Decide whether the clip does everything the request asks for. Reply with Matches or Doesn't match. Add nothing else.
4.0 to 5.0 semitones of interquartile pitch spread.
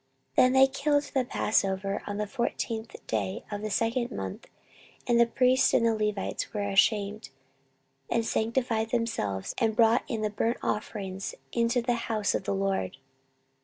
Doesn't match